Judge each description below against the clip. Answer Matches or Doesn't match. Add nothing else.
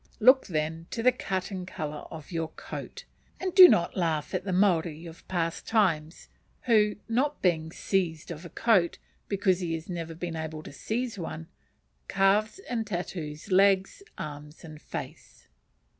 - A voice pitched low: Doesn't match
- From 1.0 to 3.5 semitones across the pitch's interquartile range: Doesn't match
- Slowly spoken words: Doesn't match